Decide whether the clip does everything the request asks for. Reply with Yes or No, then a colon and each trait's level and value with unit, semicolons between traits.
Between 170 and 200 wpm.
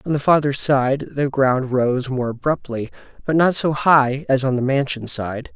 Yes: average, 195 wpm